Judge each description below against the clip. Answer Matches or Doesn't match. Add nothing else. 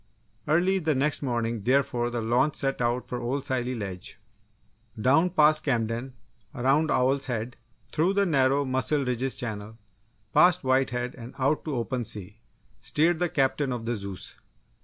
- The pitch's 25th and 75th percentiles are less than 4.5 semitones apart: Matches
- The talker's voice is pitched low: Matches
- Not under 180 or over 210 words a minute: Doesn't match